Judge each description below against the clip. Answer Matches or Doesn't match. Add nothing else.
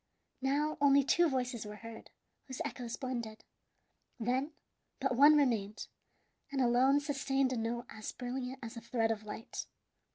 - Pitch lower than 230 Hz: Doesn't match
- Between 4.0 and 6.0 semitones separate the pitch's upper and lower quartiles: Doesn't match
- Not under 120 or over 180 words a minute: Matches